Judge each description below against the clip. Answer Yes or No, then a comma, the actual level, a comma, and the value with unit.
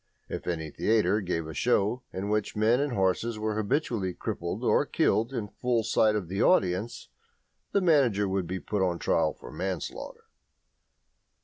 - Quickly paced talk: No, average, 170 wpm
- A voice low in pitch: Yes, low, 105 Hz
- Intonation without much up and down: No, average, 3.8 semitones